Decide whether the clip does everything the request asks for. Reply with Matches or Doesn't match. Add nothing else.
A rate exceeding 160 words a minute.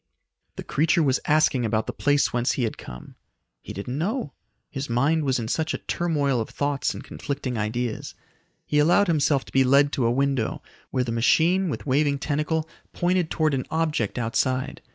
Matches